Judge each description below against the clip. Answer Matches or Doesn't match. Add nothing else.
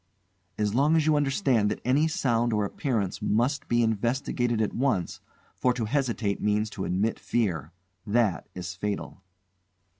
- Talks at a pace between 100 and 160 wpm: Matches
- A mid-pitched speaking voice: Doesn't match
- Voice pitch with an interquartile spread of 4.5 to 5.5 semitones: Doesn't match